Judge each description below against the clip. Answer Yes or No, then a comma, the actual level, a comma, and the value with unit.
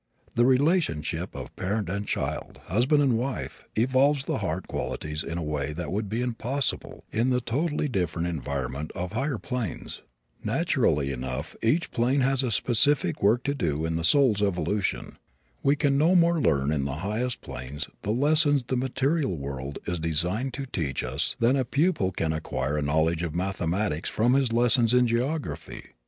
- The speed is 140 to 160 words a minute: No, average, 175 wpm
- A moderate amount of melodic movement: No, wide, 8.6 semitones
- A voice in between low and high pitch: No, low, 110 Hz